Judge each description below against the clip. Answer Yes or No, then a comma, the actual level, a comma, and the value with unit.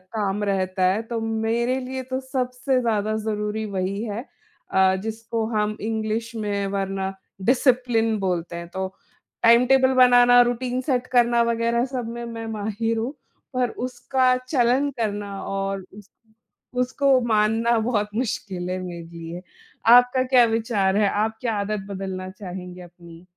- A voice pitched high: Yes, high, 220 Hz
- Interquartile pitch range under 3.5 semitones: No, average, 3.8 semitones